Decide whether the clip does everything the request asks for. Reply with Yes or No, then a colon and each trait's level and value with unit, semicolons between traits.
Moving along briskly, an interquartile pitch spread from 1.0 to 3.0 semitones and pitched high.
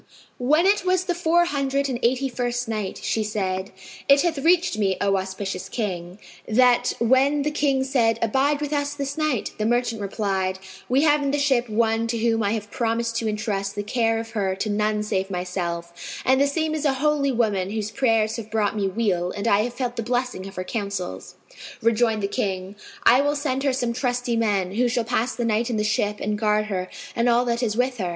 No: fast, 215 wpm; average, 4.4 semitones; high, 230 Hz